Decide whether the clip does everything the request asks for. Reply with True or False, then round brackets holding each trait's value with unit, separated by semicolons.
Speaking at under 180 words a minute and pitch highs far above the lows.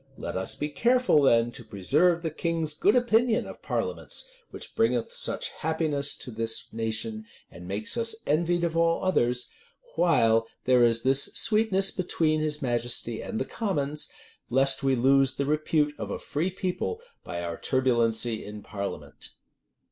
True (155 wpm; 6.9 semitones)